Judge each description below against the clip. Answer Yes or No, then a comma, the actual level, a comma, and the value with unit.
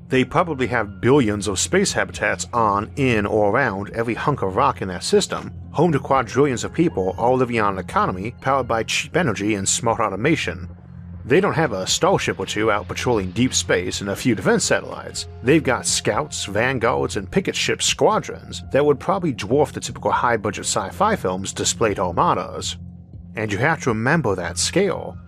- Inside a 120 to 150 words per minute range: No, average, 185 wpm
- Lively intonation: Yes, wide, 6.5 semitones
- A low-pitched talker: Yes, low, 110 Hz